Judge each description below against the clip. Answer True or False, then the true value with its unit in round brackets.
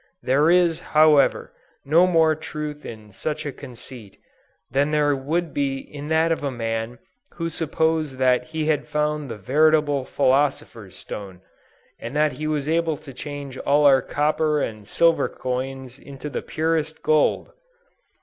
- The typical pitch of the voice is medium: True (145 Hz)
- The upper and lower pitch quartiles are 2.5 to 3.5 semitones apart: True (3.0 semitones)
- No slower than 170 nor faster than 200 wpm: False (150 wpm)